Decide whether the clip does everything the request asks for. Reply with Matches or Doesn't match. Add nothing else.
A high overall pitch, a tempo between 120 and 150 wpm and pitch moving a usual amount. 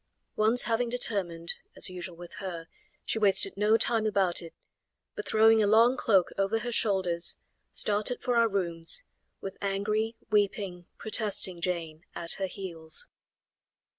Matches